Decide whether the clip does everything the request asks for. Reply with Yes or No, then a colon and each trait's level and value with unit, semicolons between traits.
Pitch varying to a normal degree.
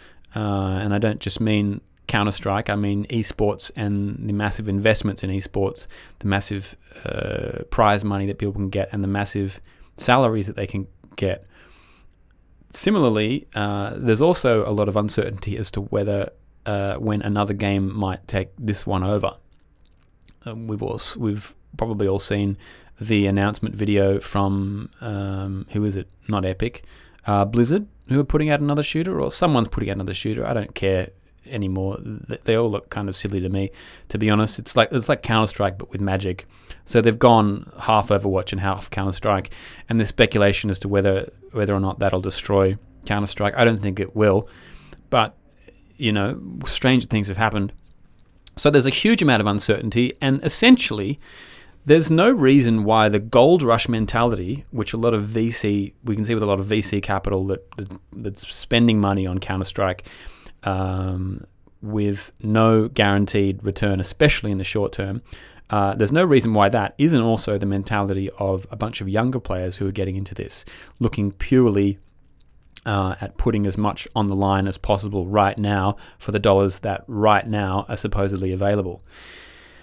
No: narrow, 2.2 semitones